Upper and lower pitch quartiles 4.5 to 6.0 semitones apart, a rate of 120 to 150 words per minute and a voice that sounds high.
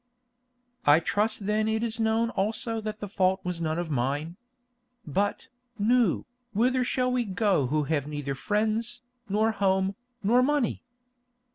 Yes: average, 5.0 semitones; average, 145 wpm; high, 210 Hz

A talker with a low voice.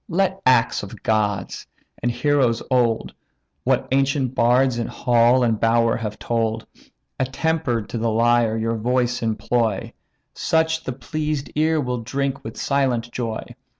Yes: low, 120 Hz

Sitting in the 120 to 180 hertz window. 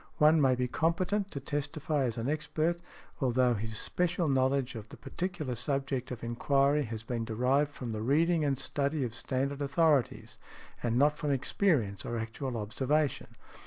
Yes: low, 135 Hz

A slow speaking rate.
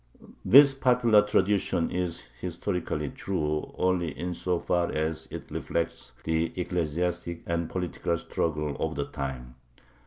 Yes: slow, 115 wpm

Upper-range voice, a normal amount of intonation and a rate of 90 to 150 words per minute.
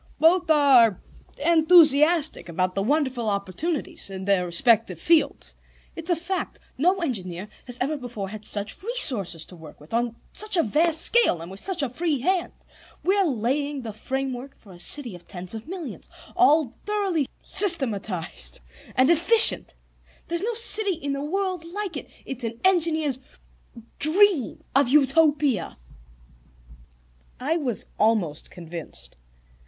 No: very high, 275 Hz; wide, 8.1 semitones; average, 140 wpm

